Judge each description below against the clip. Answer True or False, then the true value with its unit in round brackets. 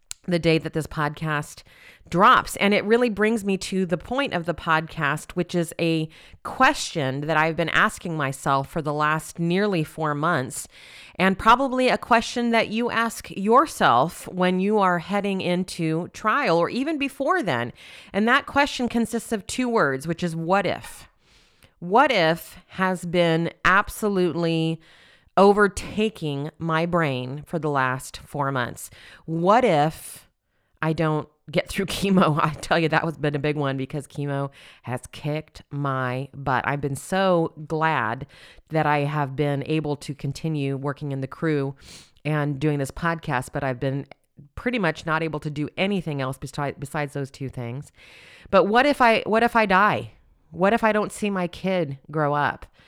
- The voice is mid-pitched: True (160 Hz)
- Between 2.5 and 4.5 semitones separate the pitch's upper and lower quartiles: False (4.9 semitones)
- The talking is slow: False (165 wpm)